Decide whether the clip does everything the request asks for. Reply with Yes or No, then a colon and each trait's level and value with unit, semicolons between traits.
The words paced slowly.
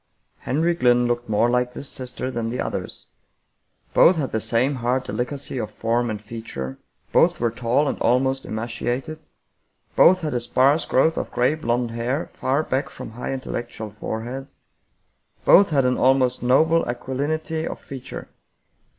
No: average, 155 wpm